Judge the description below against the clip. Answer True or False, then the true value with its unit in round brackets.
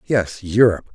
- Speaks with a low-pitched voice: True (100 Hz)